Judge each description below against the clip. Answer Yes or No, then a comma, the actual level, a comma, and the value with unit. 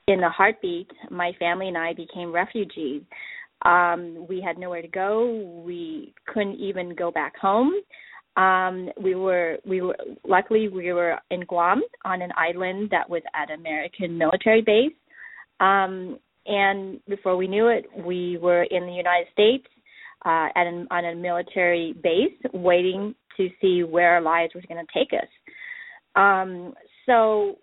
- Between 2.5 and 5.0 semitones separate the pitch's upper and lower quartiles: Yes, average, 2.8 semitones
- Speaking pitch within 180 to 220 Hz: Yes, medium, 185 Hz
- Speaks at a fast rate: No, average, 155 wpm